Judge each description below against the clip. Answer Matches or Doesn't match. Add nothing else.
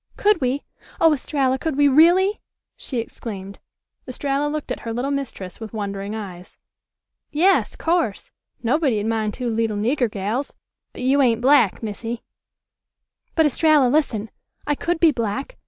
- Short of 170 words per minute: Matches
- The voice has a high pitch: Matches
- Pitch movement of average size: Matches